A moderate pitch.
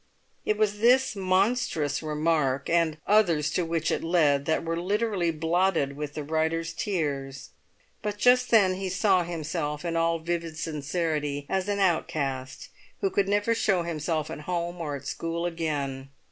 Yes: medium, 165 Hz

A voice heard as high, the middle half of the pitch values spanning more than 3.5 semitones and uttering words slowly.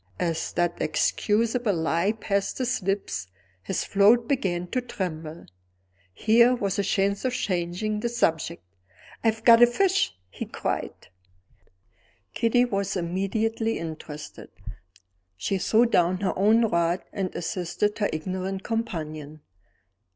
Yes: high, 195 Hz; average, 4.7 semitones; slow, 120 wpm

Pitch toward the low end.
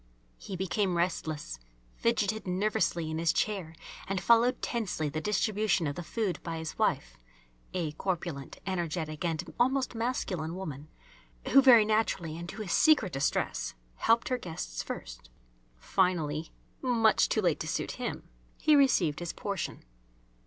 No: medium, 180 Hz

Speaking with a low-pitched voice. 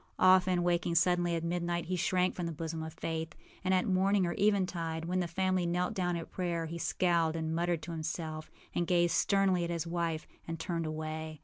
No: medium, 170 Hz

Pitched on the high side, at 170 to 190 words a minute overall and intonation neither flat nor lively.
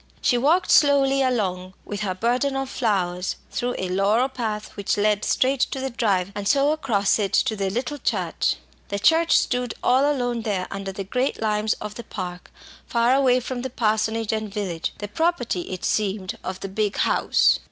Yes: high, 220 Hz; average, 185 wpm; average, 4.6 semitones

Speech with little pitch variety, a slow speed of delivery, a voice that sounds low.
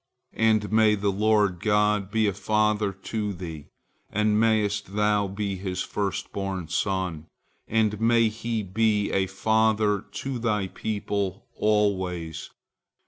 Yes: narrow, 1.9 semitones; slow, 130 wpm; low, 105 Hz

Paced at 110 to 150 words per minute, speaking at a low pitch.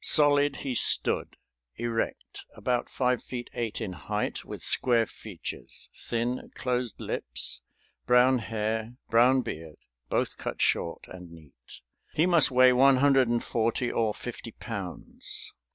Yes: slow, 135 wpm; low, 120 Hz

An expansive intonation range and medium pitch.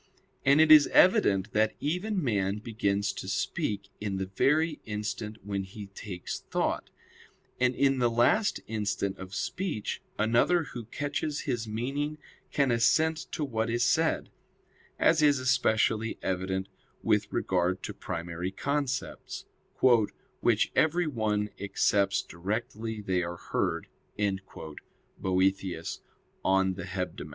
No: wide, 6.3 semitones; low, 110 Hz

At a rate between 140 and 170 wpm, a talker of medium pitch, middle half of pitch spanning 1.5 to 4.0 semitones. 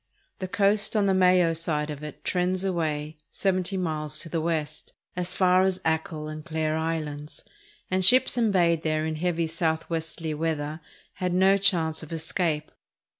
Yes: average, 160 wpm; medium, 165 Hz; average, 2.9 semitones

